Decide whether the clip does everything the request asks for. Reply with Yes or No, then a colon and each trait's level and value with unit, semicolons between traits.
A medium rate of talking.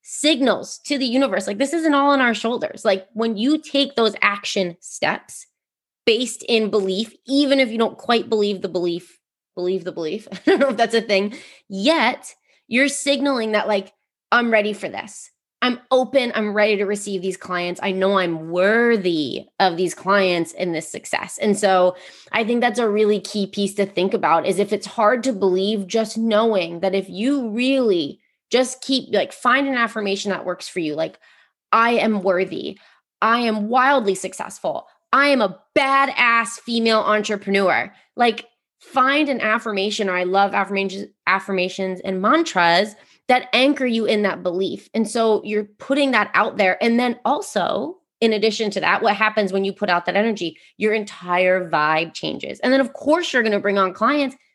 Yes: average, 185 wpm